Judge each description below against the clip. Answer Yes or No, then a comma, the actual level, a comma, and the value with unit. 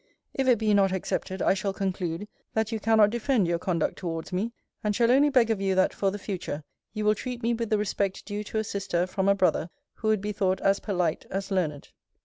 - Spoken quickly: Yes, fast, 235 wpm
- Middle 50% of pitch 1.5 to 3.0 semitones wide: Yes, average, 2.7 semitones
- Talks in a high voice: Yes, high, 200 Hz